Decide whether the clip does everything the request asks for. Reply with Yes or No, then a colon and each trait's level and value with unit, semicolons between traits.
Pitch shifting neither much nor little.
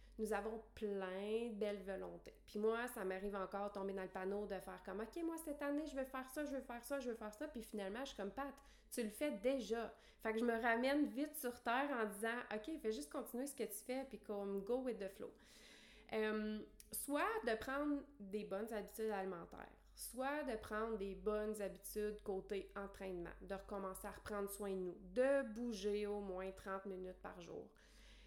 Yes: average, 4.1 semitones